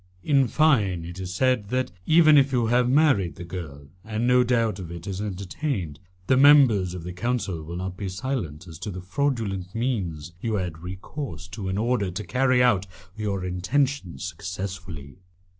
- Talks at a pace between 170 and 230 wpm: Yes, average, 180 wpm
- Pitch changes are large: Yes, wide, 5.8 semitones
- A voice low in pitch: Yes, low, 100 Hz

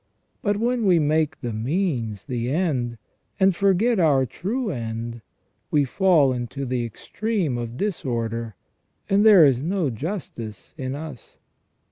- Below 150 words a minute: Yes, average, 140 wpm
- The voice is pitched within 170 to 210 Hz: No, medium, 145 Hz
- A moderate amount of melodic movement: No, wide, 8.1 semitones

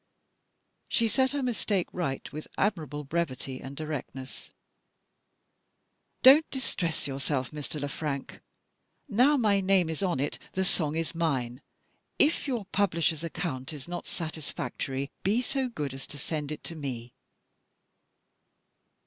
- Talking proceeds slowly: Yes, slow, 130 wpm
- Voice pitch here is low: No, medium, 160 Hz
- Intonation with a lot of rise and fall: Yes, wide, 6.0 semitones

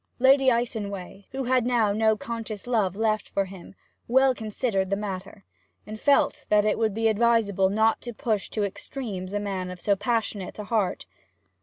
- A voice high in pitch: Yes, high, 215 Hz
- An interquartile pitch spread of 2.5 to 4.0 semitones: Yes, average, 2.8 semitones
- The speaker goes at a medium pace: Yes, average, 175 wpm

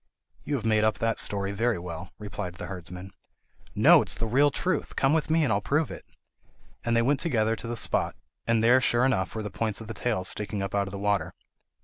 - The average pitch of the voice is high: No, low, 110 Hz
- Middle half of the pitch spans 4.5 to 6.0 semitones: No, average, 3.5 semitones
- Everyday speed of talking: No, fast, 240 wpm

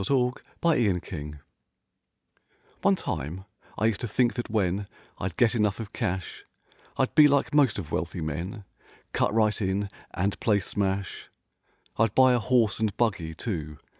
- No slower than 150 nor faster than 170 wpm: Yes, average, 155 wpm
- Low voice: Yes, low, 105 Hz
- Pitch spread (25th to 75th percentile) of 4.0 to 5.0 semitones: Yes, average, 4.4 semitones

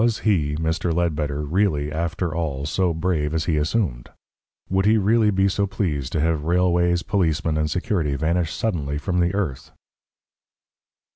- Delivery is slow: No, average, 155 wpm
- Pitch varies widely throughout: No, average, 3.8 semitones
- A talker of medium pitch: No, very low, 85 Hz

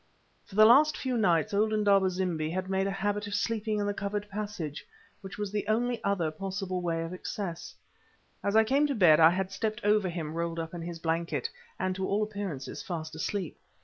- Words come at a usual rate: No, fast, 210 wpm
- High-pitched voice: Yes, high, 195 Hz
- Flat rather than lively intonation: No, average, 3.7 semitones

